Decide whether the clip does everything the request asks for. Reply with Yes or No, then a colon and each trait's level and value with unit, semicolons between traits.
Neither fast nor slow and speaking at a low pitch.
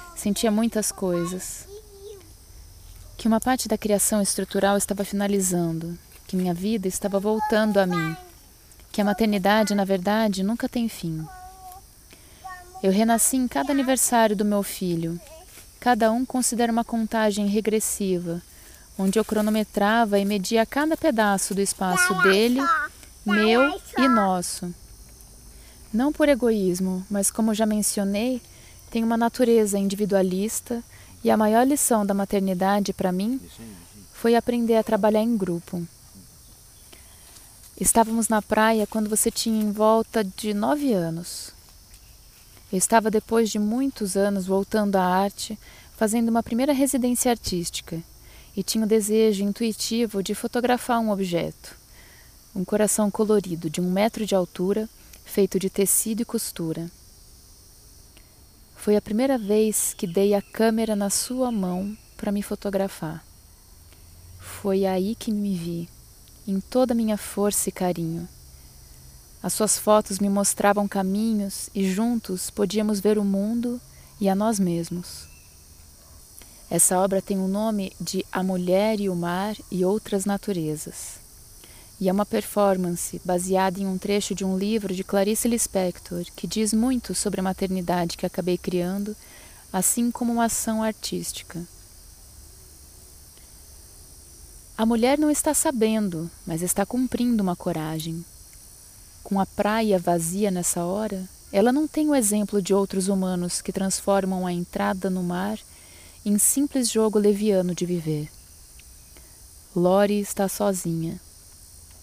No: average, 135 wpm; high, 200 Hz